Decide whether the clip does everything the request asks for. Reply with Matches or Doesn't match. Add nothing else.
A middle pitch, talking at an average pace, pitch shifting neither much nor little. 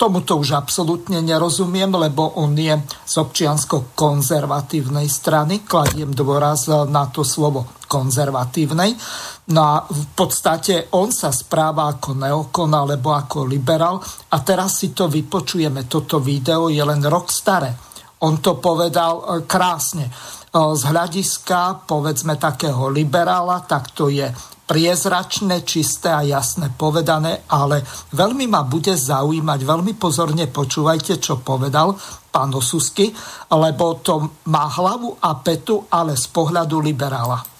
Matches